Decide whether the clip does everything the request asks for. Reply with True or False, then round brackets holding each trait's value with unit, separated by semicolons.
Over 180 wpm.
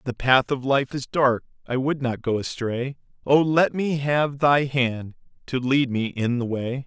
True (200 wpm)